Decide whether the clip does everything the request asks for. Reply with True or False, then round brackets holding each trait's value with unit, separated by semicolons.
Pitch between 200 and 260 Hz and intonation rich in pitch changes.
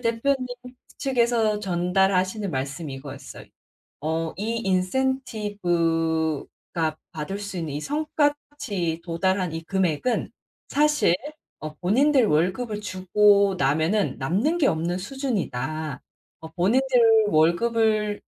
False (190 Hz; 6.0 semitones)